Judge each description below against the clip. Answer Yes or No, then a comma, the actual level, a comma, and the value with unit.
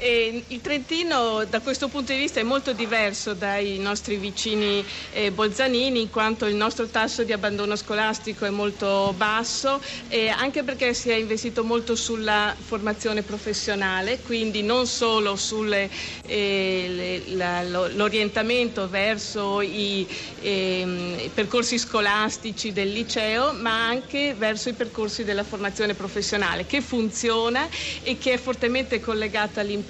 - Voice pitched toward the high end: Yes, high, 220 Hz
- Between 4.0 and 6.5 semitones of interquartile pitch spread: No, narrow, 2.5 semitones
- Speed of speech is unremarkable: Yes, average, 130 wpm